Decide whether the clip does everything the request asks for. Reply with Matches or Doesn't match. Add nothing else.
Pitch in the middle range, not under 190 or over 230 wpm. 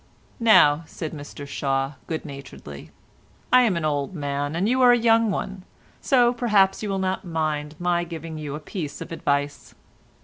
Doesn't match